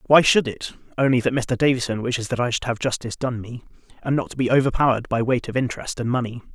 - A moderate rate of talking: No, fast, 240 wpm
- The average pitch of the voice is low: Yes, low, 125 Hz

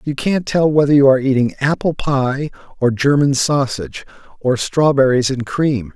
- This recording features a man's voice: Yes, male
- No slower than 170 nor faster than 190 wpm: No, average, 160 wpm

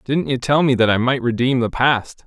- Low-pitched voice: Yes, low, 125 Hz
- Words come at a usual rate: No, fast, 265 wpm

